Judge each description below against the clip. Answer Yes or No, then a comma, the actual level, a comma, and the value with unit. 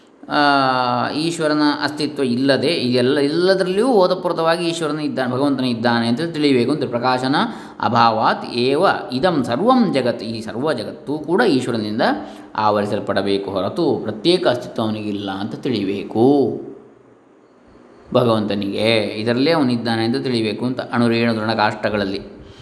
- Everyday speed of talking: No, fast, 110 wpm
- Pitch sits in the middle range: No, low, 125 Hz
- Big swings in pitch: No, average, 5.0 semitones